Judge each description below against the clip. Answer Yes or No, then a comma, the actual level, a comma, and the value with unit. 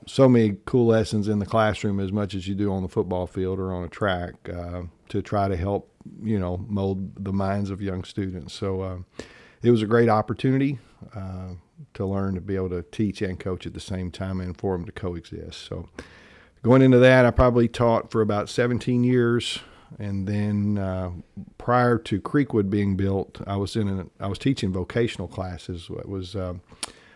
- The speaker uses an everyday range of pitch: Yes, average, 3.2 semitones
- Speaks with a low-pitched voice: Yes, low, 100 Hz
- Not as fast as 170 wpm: No, average, 200 wpm